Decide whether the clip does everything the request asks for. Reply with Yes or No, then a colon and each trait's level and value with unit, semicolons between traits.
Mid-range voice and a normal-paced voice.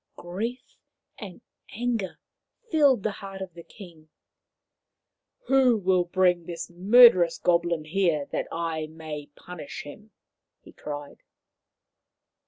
No: medium, 180 Hz; slow, 120 wpm